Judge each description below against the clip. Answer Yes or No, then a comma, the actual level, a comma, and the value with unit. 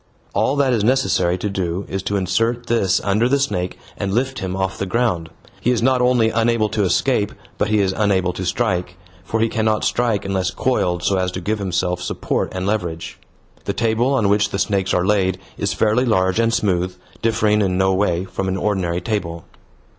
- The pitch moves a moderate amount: Yes, average, 3.5 semitones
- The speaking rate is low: No, average, 200 wpm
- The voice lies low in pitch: Yes, low, 100 Hz